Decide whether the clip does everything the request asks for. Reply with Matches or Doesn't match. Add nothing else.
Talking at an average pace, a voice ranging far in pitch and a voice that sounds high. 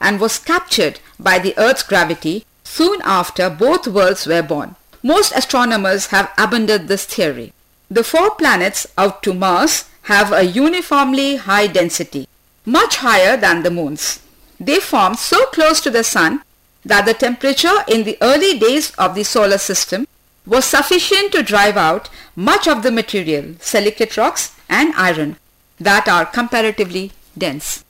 Matches